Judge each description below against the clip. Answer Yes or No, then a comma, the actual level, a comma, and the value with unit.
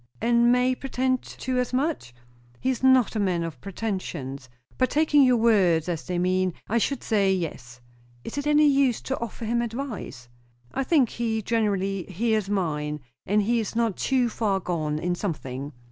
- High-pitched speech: Yes, high, 215 Hz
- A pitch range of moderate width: No, wide, 6.0 semitones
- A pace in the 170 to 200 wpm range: Yes, average, 175 wpm